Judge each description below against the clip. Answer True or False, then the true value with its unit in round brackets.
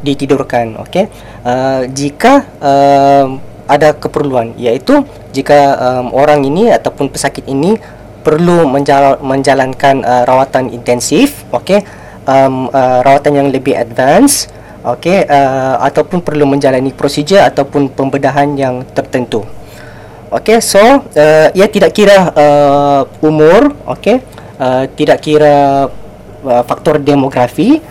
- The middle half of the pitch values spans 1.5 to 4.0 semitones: True (2.8 semitones)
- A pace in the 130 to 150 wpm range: False (115 wpm)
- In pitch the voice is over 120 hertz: True (140 Hz)